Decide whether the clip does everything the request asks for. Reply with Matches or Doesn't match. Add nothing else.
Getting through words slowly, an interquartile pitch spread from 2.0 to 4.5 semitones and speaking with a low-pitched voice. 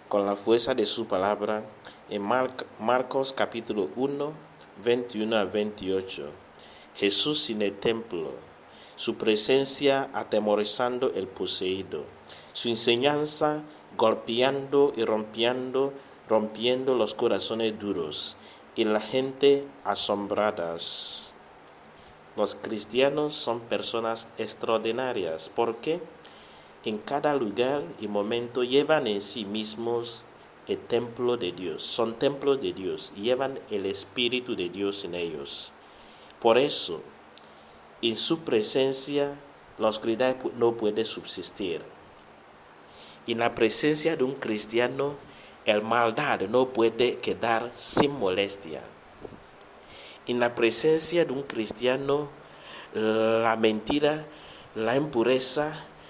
Matches